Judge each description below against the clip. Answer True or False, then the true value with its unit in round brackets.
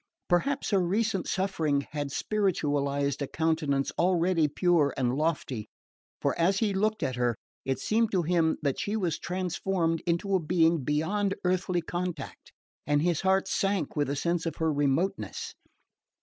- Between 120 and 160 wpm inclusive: True (155 wpm)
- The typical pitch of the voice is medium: True (170 Hz)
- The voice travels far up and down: False (4.6 semitones)